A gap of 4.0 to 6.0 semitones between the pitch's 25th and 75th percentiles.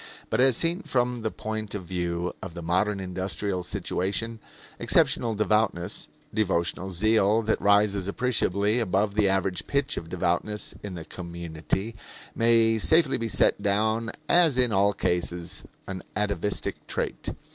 No: average, 3.6 semitones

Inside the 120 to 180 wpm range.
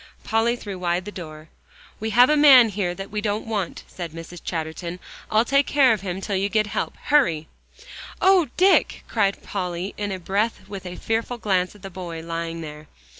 No: average, 195 wpm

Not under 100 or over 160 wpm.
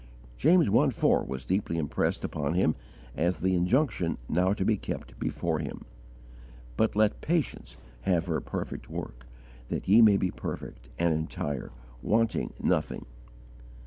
Yes: average, 145 wpm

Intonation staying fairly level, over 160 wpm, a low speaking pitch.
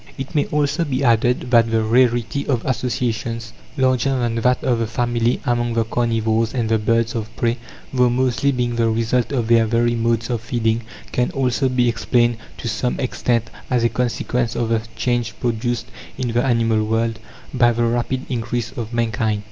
Yes: narrow, 1.5 semitones; average, 180 wpm; low, 120 Hz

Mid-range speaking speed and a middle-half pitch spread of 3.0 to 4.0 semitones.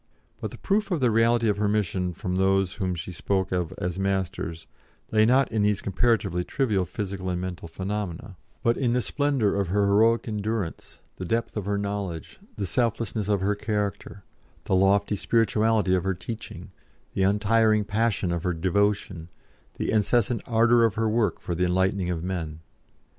Yes: average, 175 wpm; average, 3.3 semitones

